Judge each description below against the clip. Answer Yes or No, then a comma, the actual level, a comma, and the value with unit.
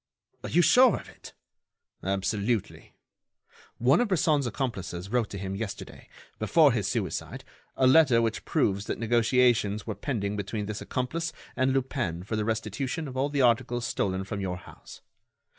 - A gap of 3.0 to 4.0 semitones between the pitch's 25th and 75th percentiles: No, average, 4.6 semitones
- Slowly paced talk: No, average, 160 wpm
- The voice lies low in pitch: Yes, low, 115 Hz